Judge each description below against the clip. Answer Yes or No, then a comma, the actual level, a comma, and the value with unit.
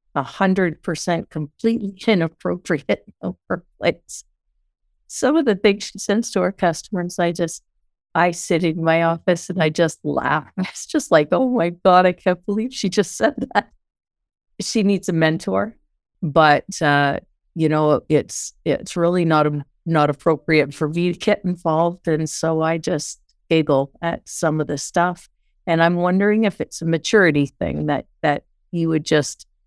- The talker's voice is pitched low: No, medium, 170 Hz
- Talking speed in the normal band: Yes, average, 165 wpm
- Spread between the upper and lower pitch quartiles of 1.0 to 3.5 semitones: Yes, average, 3.2 semitones